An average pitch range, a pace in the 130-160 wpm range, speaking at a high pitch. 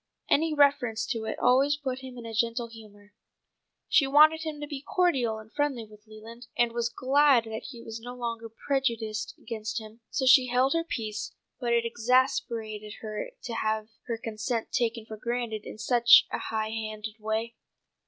No: average, 3.0 semitones; average, 180 wpm; high, 230 Hz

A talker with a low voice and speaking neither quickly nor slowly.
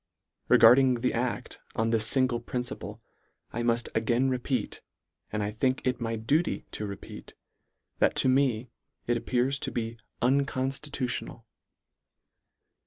No: low, 125 Hz; slow, 125 wpm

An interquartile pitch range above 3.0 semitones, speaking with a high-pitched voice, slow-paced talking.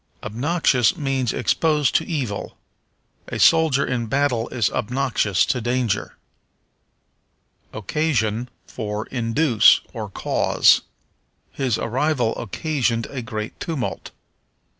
No: average, 4.1 semitones; low, 125 Hz; slow, 95 wpm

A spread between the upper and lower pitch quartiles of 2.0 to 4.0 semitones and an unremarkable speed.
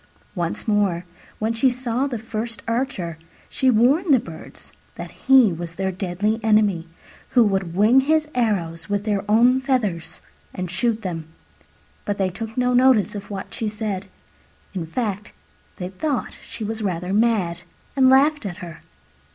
No: average, 4.8 semitones; average, 160 wpm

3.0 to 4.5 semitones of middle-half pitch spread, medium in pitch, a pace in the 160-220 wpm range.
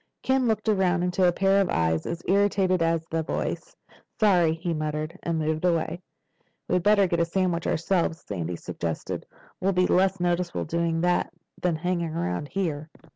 No: narrow, 2.6 semitones; medium, 175 Hz; average, 170 wpm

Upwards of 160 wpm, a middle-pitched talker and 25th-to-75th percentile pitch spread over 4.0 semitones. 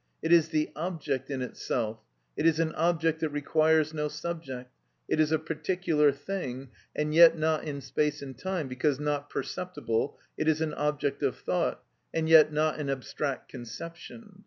No: average, 170 wpm; medium, 155 Hz; narrow, 2.4 semitones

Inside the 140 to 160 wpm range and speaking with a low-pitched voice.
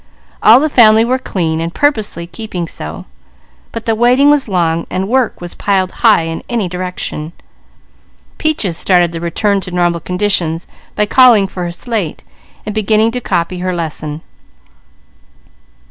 No: average, 150 wpm; high, 190 Hz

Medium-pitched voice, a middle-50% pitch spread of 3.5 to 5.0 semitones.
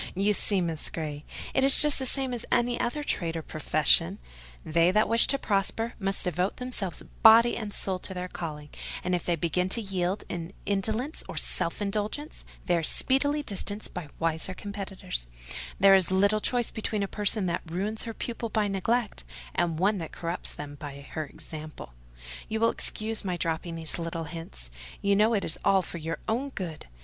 No: high, 195 Hz; average, 4.7 semitones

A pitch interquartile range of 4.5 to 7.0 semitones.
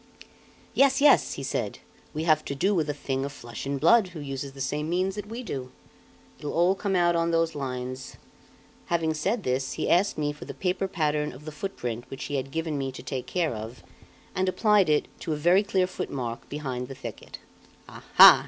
Yes: average, 5.3 semitones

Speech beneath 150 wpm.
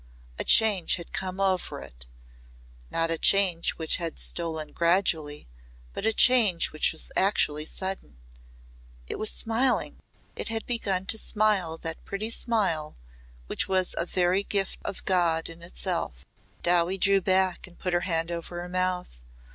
No: average, 155 wpm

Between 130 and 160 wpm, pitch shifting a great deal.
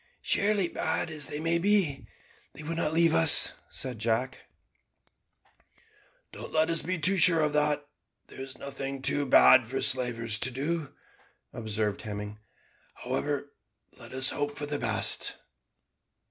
No: average, 145 wpm; average, 3.9 semitones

